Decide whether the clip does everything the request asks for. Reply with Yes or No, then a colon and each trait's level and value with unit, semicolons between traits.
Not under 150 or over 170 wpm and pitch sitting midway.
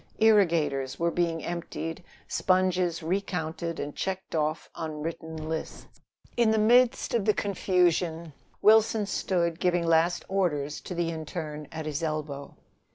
No: slow, 135 wpm; medium, 170 Hz